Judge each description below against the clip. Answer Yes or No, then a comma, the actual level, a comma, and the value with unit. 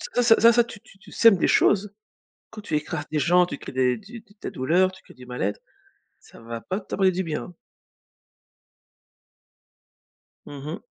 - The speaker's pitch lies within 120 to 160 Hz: No, medium, 180 Hz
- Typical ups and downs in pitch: No, wide, 6.4 semitones